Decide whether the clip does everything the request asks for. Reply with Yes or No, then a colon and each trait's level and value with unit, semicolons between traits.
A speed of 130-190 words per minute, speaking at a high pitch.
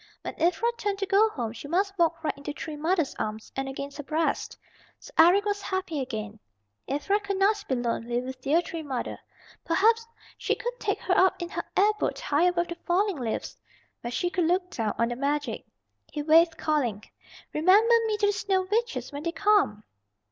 No: average, 200 wpm; very high, 330 Hz